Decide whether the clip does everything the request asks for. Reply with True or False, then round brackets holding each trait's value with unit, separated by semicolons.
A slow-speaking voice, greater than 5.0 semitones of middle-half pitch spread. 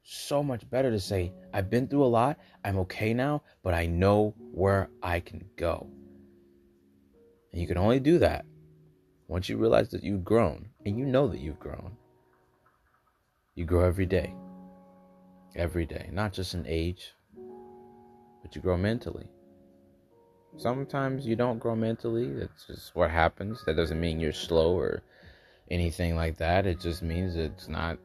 False (160 wpm; 5.5 semitones)